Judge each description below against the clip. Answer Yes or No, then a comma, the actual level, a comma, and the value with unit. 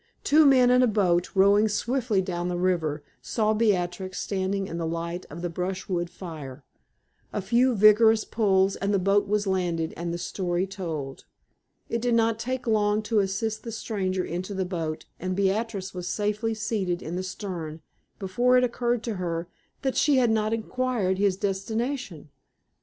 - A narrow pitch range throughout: No, average, 3.8 semitones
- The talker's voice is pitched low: No, high, 195 Hz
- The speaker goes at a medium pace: Yes, average, 170 wpm